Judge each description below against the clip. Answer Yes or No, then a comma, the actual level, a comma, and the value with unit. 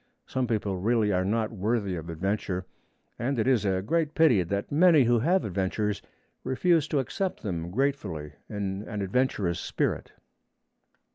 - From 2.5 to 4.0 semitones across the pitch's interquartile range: No, wide, 5.6 semitones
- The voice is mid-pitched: No, low, 105 Hz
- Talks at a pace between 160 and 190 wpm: No, average, 150 wpm